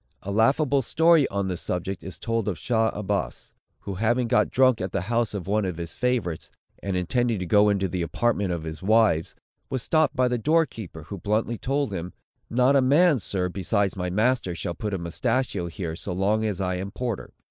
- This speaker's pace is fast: Yes, fast, 210 wpm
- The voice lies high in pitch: No, low, 105 Hz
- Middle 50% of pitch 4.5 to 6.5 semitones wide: Yes, average, 5.1 semitones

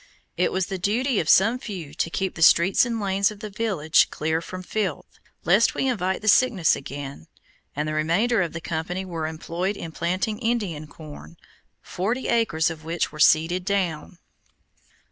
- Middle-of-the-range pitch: Yes, medium, 180 Hz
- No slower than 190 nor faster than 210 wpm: No, average, 175 wpm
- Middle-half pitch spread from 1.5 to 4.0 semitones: No, average, 4.6 semitones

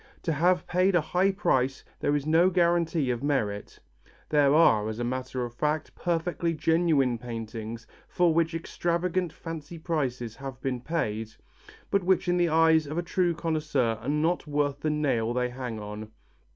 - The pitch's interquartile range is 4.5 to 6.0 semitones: Yes, average, 5.3 semitones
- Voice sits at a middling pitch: Yes, medium, 150 Hz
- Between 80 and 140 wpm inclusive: No, average, 165 wpm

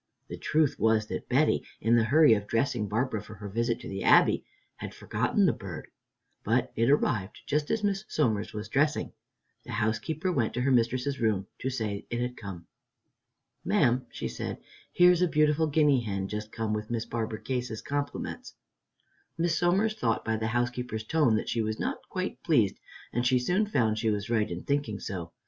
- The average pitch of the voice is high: No, low, 120 Hz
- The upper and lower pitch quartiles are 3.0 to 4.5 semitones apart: No, average, 4.9 semitones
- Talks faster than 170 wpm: Yes, average, 190 wpm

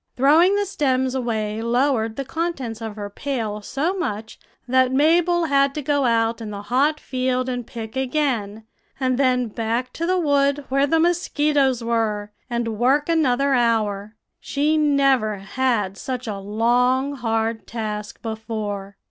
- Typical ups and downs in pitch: Yes, average, 4.1 semitones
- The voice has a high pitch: Yes, very high, 250 Hz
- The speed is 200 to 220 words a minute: No, average, 150 wpm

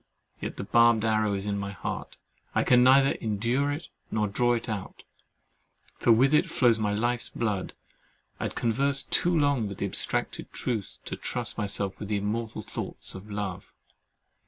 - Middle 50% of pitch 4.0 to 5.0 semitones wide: No, average, 3.2 semitones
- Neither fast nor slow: Yes, average, 165 wpm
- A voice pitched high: No, low, 110 Hz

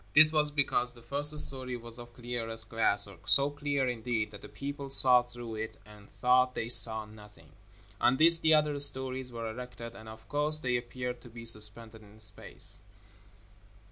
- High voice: No, low, 125 Hz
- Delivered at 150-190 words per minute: Yes, average, 175 wpm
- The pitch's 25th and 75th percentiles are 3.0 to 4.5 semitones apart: Yes, average, 3.6 semitones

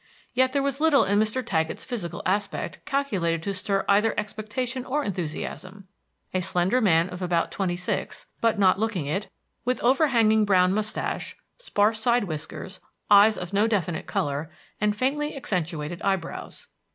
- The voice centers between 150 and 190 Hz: No, high, 205 Hz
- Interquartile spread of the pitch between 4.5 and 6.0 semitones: Yes, average, 4.8 semitones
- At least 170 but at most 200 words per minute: No, average, 150 wpm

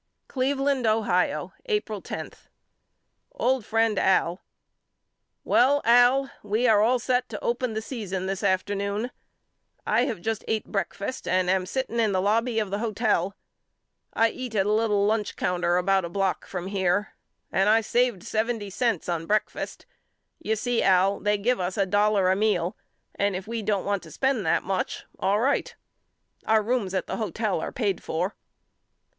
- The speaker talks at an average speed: Yes, average, 170 wpm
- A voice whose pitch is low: No, high, 210 Hz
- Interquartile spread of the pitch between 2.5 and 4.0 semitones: Yes, average, 3.3 semitones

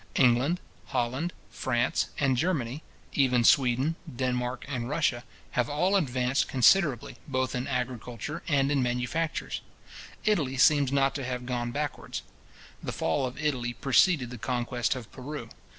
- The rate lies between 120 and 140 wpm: Yes, slow, 135 wpm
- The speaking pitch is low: Yes, low, 130 Hz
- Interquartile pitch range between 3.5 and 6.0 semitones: No, average, 2.9 semitones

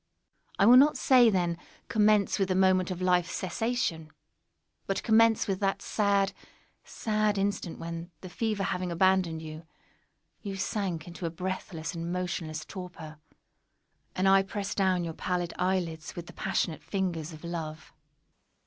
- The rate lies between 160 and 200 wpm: No, average, 145 wpm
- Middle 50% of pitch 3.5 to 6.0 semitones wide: No, average, 2.8 semitones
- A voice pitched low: No, medium, 185 Hz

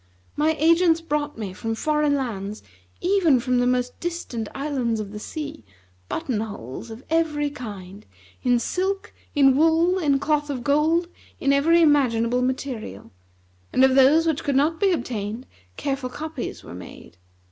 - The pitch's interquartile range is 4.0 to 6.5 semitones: Yes, average, 5.2 semitones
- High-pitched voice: Yes, very high, 275 Hz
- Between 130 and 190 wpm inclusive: Yes, average, 155 wpm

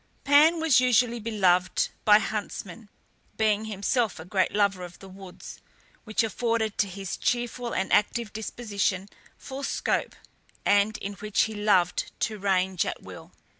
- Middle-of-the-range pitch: No, high, 210 Hz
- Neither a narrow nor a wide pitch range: Yes, average, 3.2 semitones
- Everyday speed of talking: Yes, average, 145 wpm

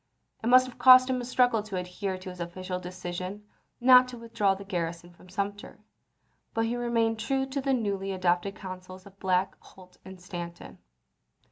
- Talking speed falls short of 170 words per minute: No, average, 175 wpm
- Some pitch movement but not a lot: Yes, average, 4.4 semitones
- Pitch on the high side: Yes, high, 195 Hz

